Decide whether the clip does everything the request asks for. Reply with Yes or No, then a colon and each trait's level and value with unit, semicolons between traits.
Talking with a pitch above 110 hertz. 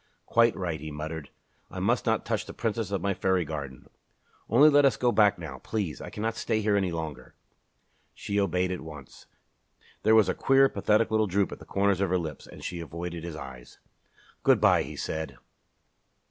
No: very low, 95 Hz